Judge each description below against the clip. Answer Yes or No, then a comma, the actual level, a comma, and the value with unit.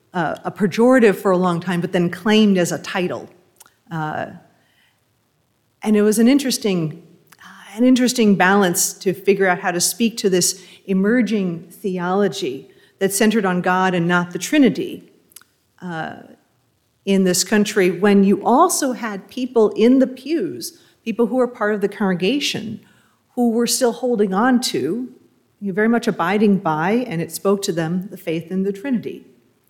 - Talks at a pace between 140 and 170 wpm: Yes, average, 165 wpm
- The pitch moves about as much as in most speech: Yes, average, 4.2 semitones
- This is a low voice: No, high, 195 Hz